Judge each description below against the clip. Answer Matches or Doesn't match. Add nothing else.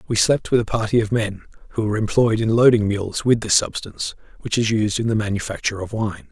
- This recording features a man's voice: Matches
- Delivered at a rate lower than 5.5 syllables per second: Doesn't match